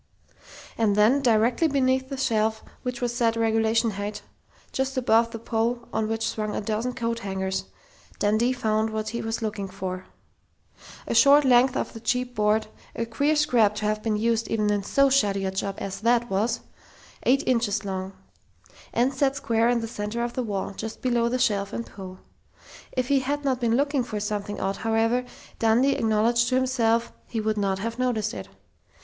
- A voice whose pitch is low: No, high, 225 Hz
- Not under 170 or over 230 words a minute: Yes, average, 190 wpm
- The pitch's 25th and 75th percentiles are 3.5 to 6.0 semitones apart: No, average, 2.7 semitones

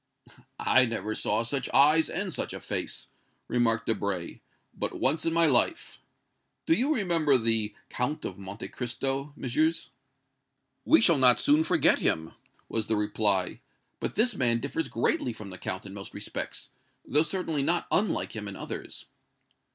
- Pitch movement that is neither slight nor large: No, wide, 6.7 semitones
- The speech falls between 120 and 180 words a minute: Yes, average, 160 wpm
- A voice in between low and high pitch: No, low, 125 Hz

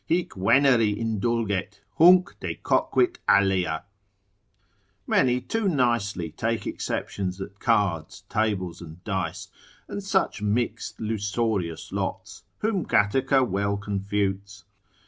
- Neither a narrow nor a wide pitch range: Yes, average, 3.4 semitones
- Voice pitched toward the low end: Yes, low, 100 Hz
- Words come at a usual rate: No, slow, 95 wpm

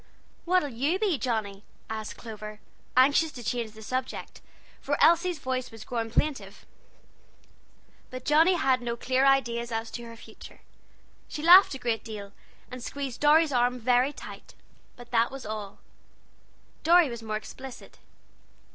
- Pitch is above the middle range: Yes, very high, 250 Hz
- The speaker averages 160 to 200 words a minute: No, average, 145 wpm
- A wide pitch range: No, average, 4.1 semitones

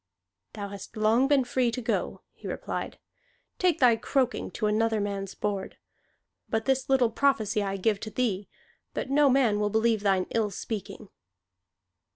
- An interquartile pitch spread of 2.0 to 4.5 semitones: Yes, average, 3.6 semitones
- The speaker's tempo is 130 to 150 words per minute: No, average, 160 wpm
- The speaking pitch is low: No, high, 220 Hz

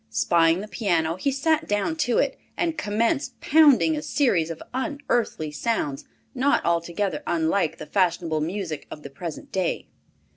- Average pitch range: No, wide, 8.6 semitones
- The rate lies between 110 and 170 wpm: Yes, average, 150 wpm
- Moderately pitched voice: No, high, 195 Hz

